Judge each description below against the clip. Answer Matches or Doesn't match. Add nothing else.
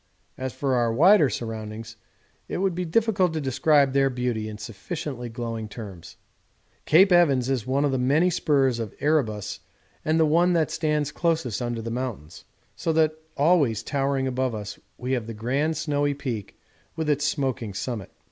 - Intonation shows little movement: Doesn't match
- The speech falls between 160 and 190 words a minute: Matches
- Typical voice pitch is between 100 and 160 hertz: Matches